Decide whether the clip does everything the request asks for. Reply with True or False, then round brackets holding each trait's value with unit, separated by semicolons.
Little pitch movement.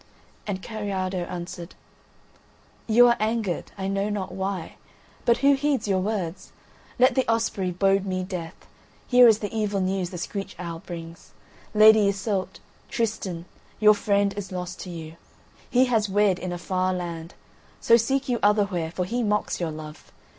False (3.2 semitones)